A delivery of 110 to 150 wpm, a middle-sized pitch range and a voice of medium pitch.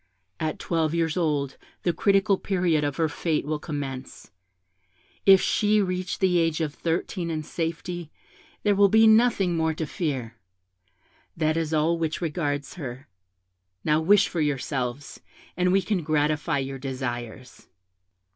Yes: average, 145 wpm; average, 3.7 semitones; medium, 160 Hz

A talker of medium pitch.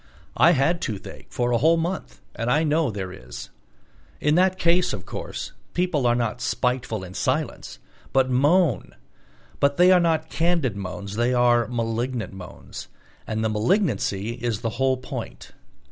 No: low, 125 Hz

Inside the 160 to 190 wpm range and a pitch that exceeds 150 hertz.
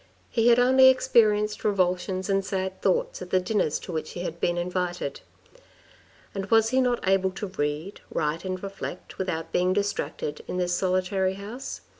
Yes: average, 170 wpm; high, 190 Hz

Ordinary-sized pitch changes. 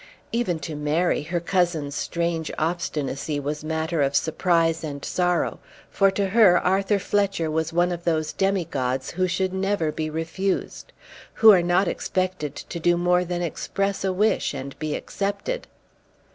Yes: average, 3.3 semitones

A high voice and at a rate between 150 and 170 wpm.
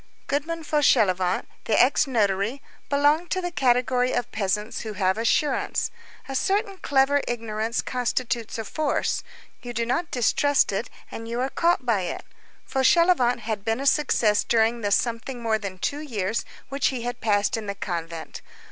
Yes: high, 240 Hz; average, 165 wpm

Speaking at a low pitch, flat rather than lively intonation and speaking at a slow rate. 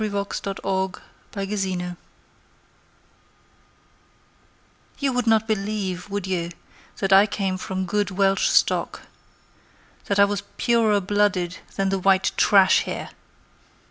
No: high, 195 Hz; narrow, 1.6 semitones; slow, 110 wpm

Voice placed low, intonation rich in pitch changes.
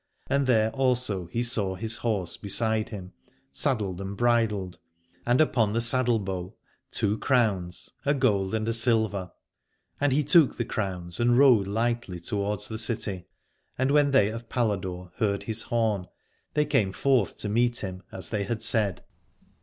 No: low, 110 Hz; average, 3.8 semitones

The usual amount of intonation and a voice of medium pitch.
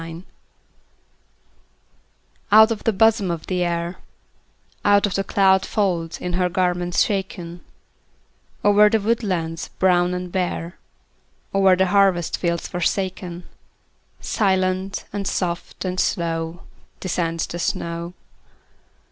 No: narrow, 2.3 semitones; medium, 180 Hz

